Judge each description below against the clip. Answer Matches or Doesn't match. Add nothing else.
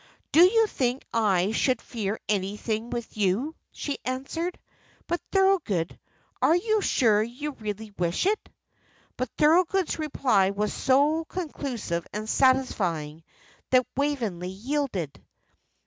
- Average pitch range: Doesn't match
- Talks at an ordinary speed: Doesn't match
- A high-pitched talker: Matches